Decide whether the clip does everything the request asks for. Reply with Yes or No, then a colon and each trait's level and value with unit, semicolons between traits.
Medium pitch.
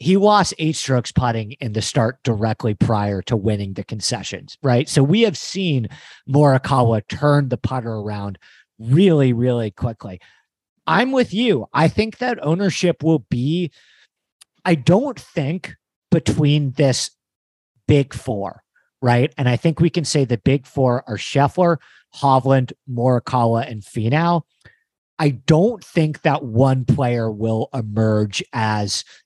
No: low, 130 Hz